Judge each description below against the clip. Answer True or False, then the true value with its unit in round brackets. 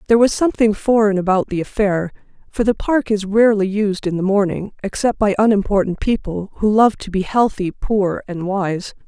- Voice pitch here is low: False (205 Hz)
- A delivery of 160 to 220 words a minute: True (185 wpm)